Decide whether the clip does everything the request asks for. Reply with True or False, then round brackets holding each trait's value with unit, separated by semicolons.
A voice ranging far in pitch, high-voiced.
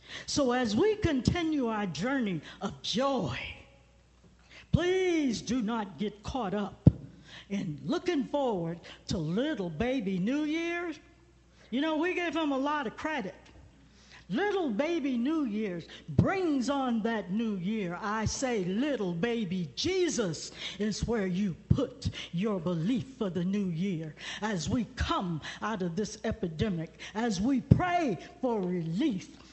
True (7.0 semitones; 225 Hz)